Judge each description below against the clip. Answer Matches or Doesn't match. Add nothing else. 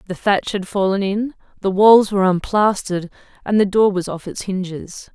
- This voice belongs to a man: Doesn't match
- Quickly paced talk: Doesn't match